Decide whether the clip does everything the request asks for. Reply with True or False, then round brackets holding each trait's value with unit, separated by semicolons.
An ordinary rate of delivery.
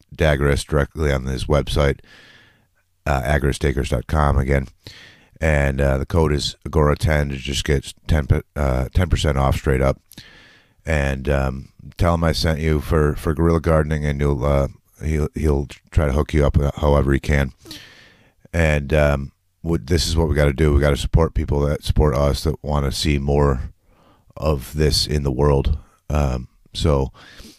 True (170 wpm)